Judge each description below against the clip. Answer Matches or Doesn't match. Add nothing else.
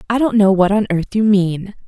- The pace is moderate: Doesn't match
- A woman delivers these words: Matches